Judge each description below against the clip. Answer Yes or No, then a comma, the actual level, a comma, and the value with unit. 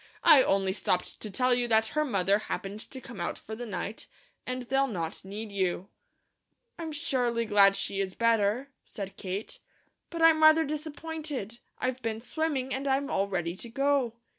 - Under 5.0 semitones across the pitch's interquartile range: No, wide, 5.6 semitones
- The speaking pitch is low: No, high, 235 Hz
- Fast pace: No, average, 175 wpm